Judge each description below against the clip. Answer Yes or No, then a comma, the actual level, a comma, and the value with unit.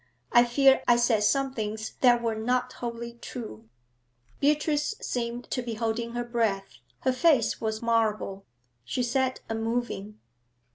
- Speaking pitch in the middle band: No, high, 235 Hz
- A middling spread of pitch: No, narrow, 2.3 semitones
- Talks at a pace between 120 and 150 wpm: Yes, average, 140 wpm